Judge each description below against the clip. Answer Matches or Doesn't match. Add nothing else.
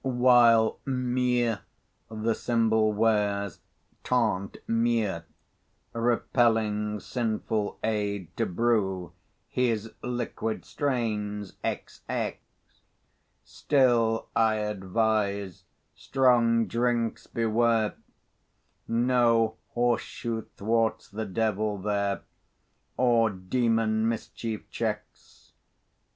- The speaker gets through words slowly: Matches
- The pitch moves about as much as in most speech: Doesn't match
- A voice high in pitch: Doesn't match